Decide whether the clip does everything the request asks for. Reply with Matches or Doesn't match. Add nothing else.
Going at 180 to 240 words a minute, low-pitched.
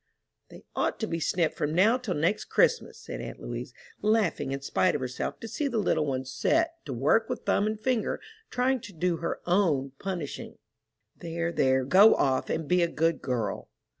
Doesn't match